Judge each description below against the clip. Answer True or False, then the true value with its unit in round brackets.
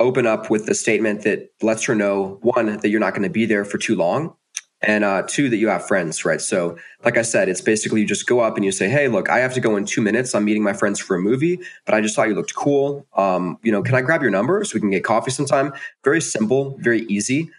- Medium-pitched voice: False (105 Hz)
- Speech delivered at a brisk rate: True (280 wpm)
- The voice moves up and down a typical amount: True (4.1 semitones)